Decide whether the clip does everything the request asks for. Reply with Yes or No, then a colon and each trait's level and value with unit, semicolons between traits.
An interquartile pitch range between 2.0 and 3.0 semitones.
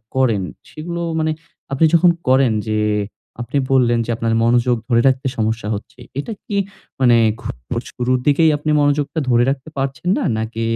No: average, 3.7 semitones